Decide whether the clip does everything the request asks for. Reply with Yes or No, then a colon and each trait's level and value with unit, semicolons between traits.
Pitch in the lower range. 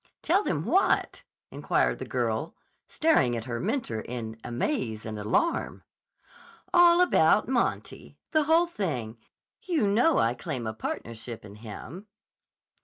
Yes: low, 130 Hz